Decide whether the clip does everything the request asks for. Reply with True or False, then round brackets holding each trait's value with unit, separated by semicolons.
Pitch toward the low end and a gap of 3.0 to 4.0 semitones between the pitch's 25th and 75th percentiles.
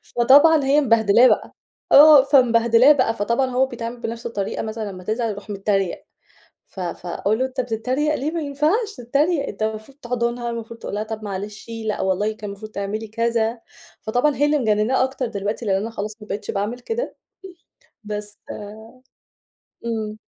False (230 Hz; 3.7 semitones)